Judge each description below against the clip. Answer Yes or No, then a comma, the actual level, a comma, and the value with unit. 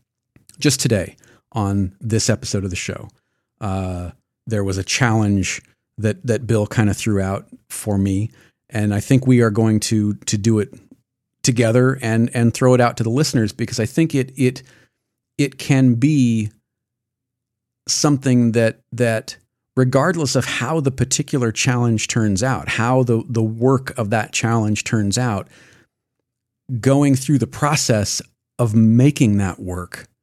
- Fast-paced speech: No, average, 155 wpm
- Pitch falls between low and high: No, low, 120 Hz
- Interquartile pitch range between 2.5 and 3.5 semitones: Yes, average, 3.1 semitones